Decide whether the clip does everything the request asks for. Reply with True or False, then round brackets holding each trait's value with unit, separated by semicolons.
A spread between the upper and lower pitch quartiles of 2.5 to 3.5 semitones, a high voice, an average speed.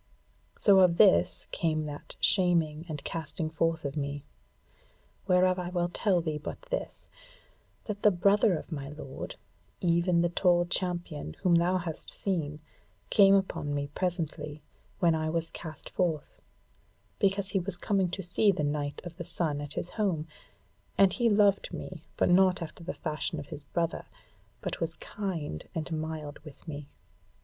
False (3.2 semitones; 170 Hz; 160 wpm)